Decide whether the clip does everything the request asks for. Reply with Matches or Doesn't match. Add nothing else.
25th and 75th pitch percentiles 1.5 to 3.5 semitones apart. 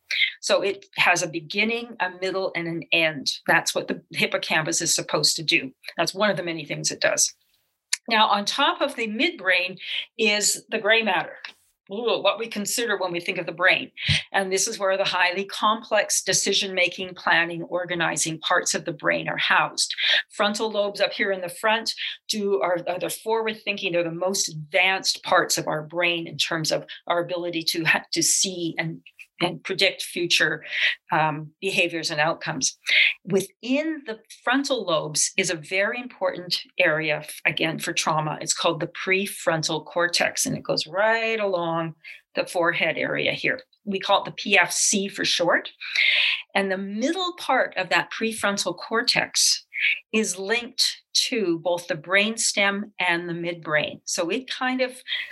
Doesn't match